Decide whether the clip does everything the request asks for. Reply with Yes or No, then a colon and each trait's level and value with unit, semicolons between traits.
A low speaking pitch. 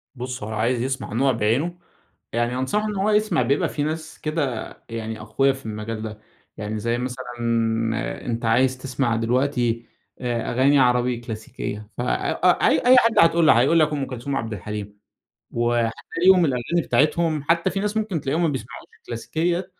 Yes: low, 130 Hz